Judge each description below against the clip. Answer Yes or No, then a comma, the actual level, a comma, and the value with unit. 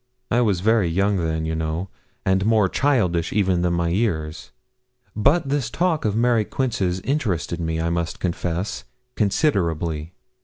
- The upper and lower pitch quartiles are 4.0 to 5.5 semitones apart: Yes, average, 5.1 semitones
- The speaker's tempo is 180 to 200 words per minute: No, average, 150 wpm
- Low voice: Yes, very low, 95 Hz